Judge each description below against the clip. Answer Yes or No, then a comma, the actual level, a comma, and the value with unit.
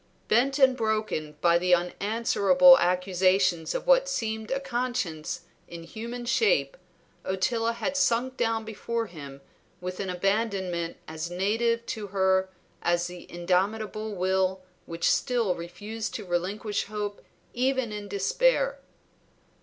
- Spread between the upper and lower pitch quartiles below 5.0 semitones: Yes, average, 4.4 semitones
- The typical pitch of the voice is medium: No, high, 205 Hz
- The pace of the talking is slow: Yes, slow, 125 wpm